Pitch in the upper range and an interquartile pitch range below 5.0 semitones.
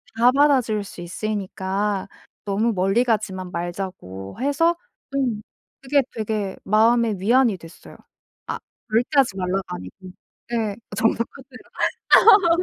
Yes: high, 215 Hz; average, 4.1 semitones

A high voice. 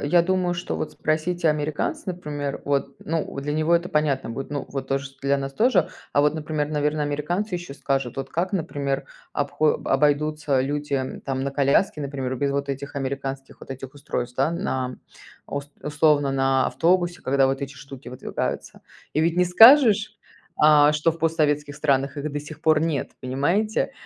No: medium, 145 Hz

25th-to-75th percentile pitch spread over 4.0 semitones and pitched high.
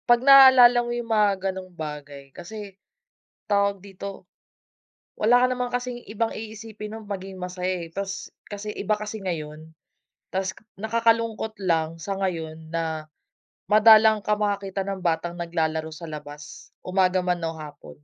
Yes: average, 4.6 semitones; high, 195 Hz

